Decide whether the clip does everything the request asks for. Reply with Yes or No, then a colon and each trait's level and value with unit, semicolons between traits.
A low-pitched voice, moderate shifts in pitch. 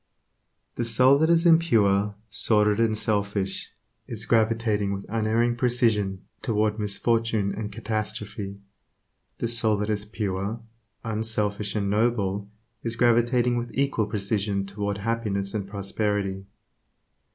No: low, 110 Hz; narrow, 2.2 semitones